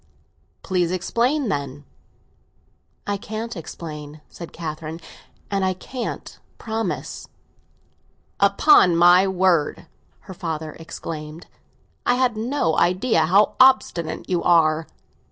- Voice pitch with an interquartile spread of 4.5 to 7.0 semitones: Yes, average, 5.1 semitones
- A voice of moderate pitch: Yes, medium, 180 Hz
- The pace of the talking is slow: Yes, slow, 100 wpm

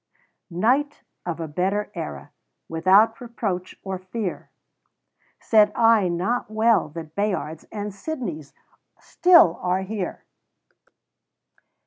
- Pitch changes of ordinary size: Yes, average, 4.2 semitones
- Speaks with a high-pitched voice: Yes, high, 195 Hz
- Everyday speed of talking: No, slow, 100 wpm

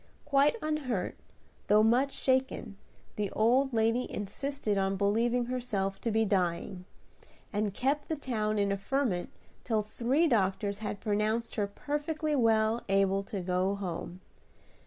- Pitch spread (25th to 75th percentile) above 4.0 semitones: Yes, average, 4.4 semitones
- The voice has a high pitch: Yes, high, 220 Hz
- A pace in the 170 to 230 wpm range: No, slow, 135 wpm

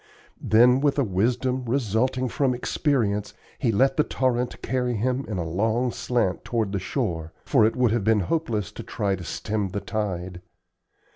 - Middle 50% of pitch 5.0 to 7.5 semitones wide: No, average, 4.1 semitones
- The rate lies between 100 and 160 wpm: No, average, 170 wpm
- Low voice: Yes, low, 115 Hz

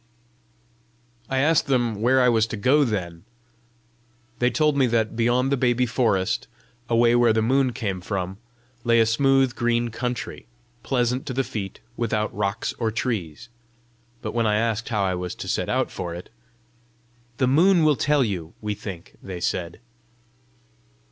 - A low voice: Yes, low, 115 Hz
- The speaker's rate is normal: Yes, average, 160 wpm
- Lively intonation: No, average, 3.7 semitones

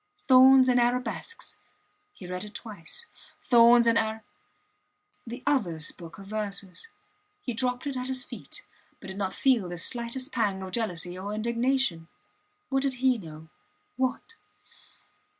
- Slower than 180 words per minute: Yes, average, 145 wpm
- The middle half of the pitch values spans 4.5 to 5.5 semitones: Yes, average, 5.0 semitones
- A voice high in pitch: Yes, high, 230 Hz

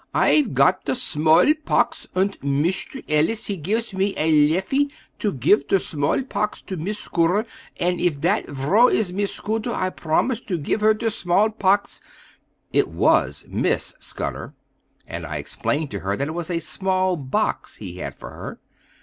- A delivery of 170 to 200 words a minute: Yes, average, 175 wpm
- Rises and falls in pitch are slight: No, average, 5.3 semitones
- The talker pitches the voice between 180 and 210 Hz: Yes, medium, 185 Hz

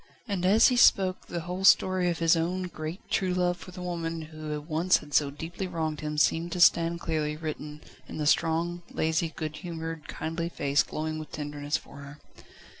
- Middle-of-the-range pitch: Yes, medium, 165 Hz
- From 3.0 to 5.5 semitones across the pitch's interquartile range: No, narrow, 2.4 semitones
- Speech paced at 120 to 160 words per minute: No, average, 190 wpm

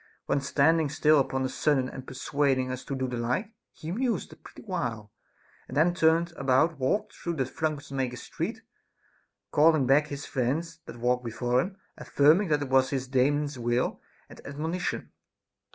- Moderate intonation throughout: Yes, average, 3.7 semitones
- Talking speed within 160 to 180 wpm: Yes, average, 170 wpm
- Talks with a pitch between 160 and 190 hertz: No, medium, 140 Hz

